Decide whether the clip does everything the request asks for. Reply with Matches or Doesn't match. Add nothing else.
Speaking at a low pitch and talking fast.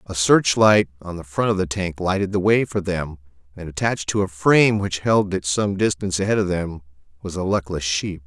Matches